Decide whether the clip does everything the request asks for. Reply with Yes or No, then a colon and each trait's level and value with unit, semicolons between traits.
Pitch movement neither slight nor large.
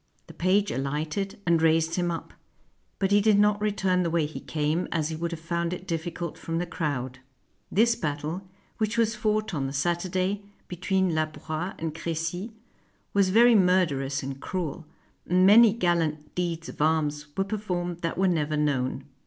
Yes: average, 3.6 semitones